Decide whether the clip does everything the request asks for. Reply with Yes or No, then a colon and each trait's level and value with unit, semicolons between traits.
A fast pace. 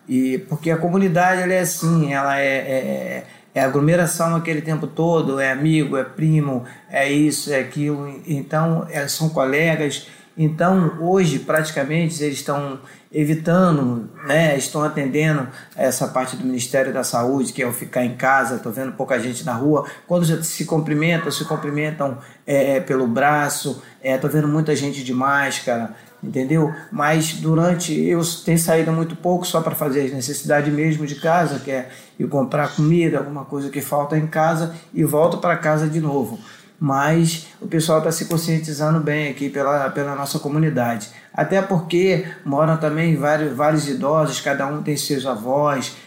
No: average, 160 wpm